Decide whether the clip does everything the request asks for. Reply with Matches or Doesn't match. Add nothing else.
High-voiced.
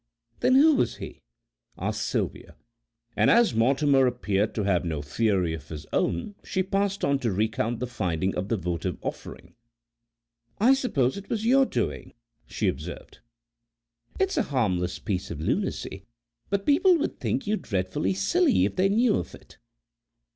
Doesn't match